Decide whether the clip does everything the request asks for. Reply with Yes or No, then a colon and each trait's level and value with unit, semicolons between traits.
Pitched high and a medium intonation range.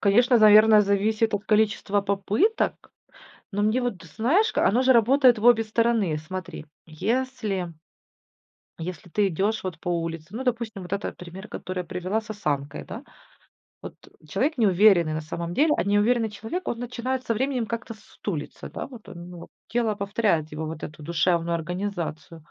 Yes: high, 205 Hz; average, 4.8 semitones